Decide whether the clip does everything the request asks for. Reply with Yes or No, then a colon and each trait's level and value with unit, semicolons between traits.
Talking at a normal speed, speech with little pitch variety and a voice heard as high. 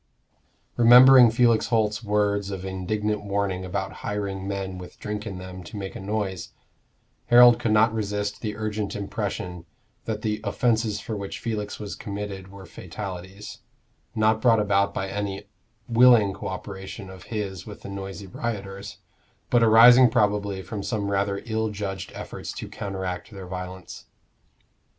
No: average, 150 wpm; narrow, 2.0 semitones; low, 100 Hz